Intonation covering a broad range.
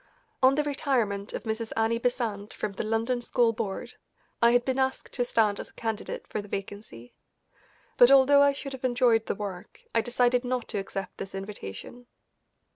No: average, 3.5 semitones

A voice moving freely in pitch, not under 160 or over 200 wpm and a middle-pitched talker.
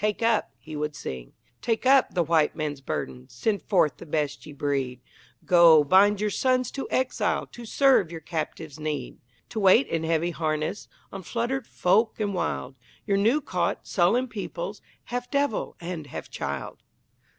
Yes: wide, 6.9 semitones; average, 165 wpm; medium, 180 Hz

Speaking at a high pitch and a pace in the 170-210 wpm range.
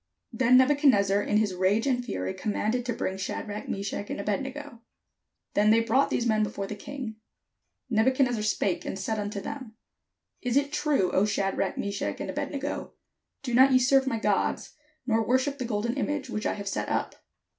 Yes: high, 225 Hz; average, 190 wpm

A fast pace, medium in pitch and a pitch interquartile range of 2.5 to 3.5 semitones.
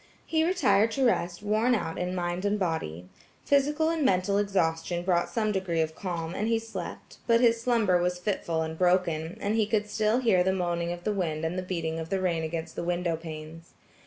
No: fast, 210 wpm; medium, 180 Hz; average, 4.3 semitones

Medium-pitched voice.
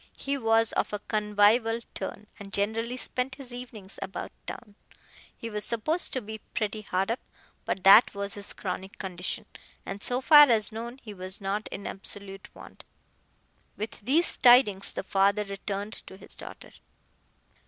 No: high, 210 Hz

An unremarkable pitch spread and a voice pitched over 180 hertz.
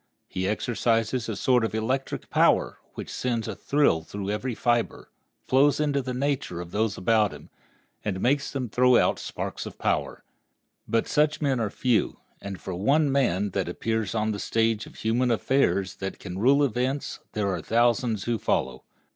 No: average, 4.2 semitones; low, 115 Hz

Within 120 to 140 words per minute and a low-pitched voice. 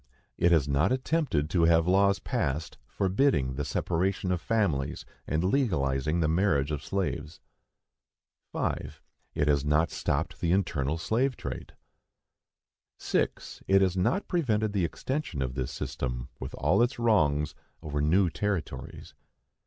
Yes: slow, 135 wpm; very low, 85 Hz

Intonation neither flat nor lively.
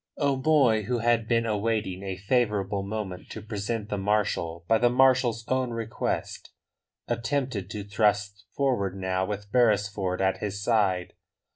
Yes: average, 3.0 semitones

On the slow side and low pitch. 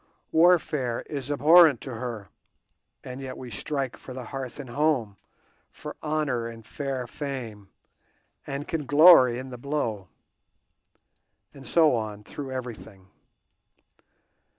Yes: slow, 125 wpm; low, 130 Hz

